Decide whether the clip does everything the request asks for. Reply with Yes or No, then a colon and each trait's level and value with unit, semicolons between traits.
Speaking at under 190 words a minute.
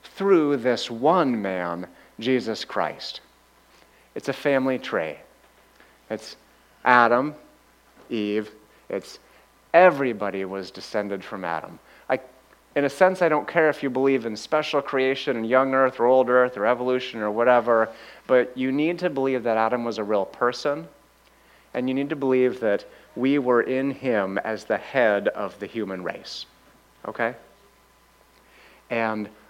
Yes: average, 145 wpm